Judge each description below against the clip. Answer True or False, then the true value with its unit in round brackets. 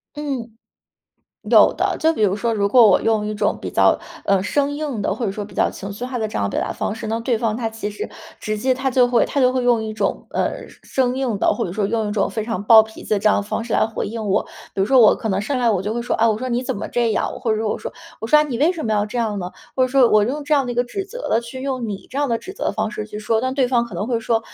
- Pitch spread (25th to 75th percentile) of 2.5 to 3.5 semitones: True (3.2 semitones)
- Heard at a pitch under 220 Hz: False (225 Hz)